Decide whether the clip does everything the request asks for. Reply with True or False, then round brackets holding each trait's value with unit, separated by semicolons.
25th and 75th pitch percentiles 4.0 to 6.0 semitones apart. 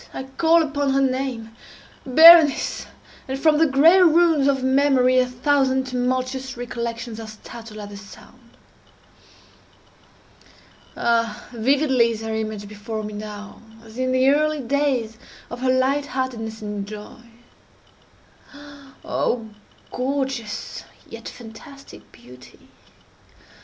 False (3.6 semitones)